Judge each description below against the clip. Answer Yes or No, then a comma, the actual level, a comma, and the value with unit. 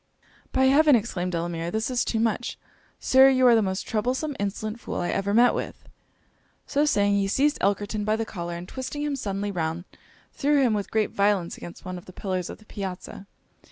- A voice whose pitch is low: No, high, 210 Hz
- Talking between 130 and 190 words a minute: No, average, 200 wpm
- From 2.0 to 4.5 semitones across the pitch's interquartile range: No, average, 5.0 semitones